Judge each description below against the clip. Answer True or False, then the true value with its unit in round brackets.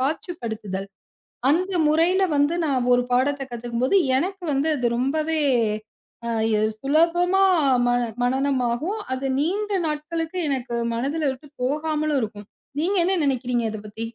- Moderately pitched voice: False (280 Hz)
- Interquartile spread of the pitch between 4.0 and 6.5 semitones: True (4.9 semitones)